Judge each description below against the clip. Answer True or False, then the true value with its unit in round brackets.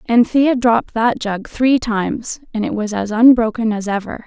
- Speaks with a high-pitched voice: True (225 Hz)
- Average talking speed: True (185 wpm)